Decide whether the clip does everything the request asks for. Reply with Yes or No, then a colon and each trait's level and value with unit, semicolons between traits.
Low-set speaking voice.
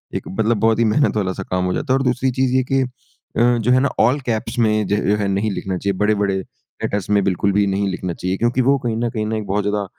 Yes: low, 105 Hz